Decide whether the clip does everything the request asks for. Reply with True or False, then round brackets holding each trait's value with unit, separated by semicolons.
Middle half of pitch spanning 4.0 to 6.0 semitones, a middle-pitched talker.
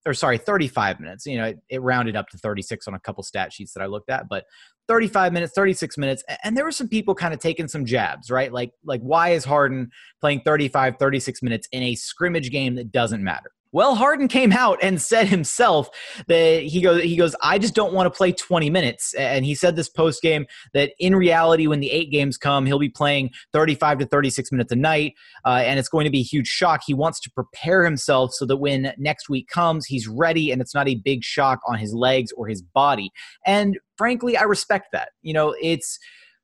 True (5.1 semitones; 150 Hz)